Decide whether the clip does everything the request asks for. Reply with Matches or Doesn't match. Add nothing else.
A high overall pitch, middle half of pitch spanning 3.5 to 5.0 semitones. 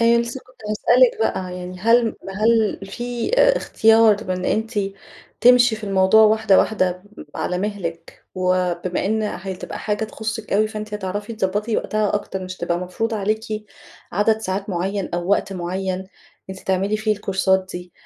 Doesn't match